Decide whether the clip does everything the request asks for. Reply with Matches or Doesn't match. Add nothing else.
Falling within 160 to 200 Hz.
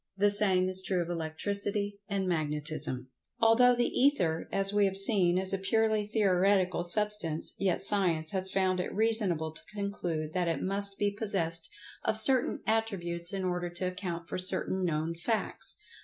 Matches